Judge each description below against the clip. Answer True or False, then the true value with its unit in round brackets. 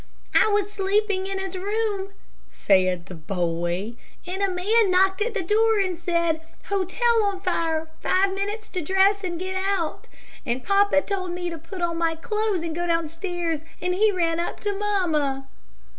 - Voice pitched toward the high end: True (370 Hz)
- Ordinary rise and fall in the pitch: True (3.4 semitones)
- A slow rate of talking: False (175 wpm)